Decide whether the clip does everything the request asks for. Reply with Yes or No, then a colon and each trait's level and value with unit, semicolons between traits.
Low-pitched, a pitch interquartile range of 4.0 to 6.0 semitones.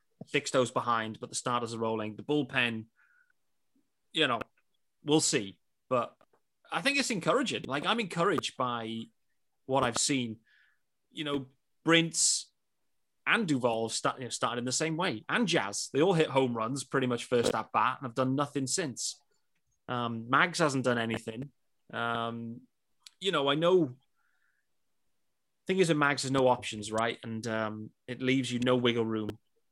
Yes: low, 130 Hz; average, 4.4 semitones